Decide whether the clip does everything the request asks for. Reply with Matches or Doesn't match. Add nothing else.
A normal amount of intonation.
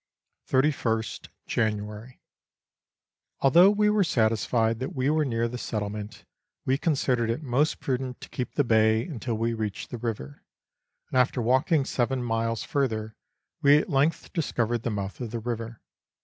Matches